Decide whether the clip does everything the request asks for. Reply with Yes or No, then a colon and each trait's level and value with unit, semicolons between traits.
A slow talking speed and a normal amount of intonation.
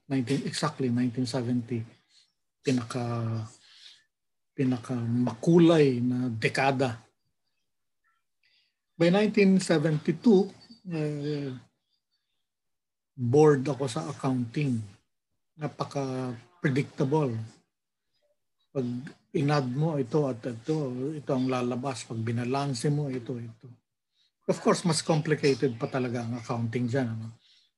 Yes: slow, 90 wpm; average, 3.7 semitones